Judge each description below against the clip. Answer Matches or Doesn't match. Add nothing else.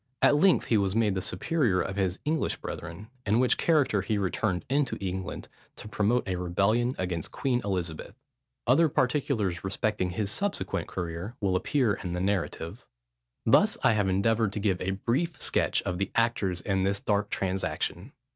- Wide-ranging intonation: Doesn't match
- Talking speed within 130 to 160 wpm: Doesn't match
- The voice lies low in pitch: Matches